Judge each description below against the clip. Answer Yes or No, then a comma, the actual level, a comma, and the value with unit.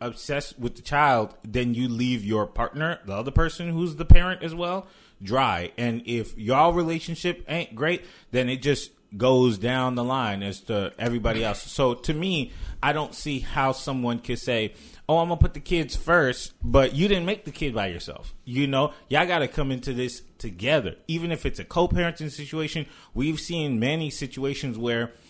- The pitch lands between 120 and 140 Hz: Yes, low, 135 Hz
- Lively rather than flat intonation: No, average, 5.0 semitones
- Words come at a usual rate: Yes, average, 185 wpm